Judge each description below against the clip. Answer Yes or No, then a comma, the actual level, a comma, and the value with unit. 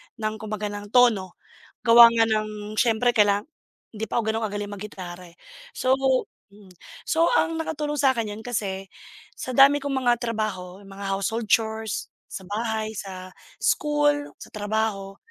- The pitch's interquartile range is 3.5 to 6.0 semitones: No, average, 2.9 semitones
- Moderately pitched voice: No, high, 220 Hz